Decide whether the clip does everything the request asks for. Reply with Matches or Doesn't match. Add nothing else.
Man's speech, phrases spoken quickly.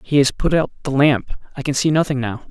Matches